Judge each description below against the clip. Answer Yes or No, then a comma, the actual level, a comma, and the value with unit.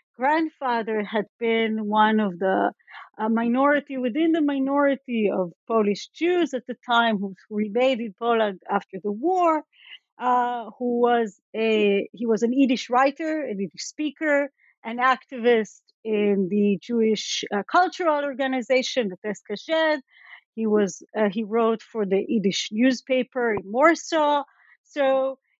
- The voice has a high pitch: Yes, high, 235 Hz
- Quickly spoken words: No, slow, 135 wpm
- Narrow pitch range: No, average, 4.3 semitones